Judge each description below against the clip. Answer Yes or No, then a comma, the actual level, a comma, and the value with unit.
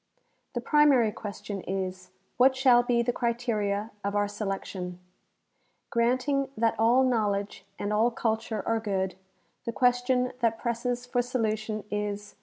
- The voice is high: Yes, high, 225 Hz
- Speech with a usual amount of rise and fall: Yes, average, 3.1 semitones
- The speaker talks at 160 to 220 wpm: No, slow, 135 wpm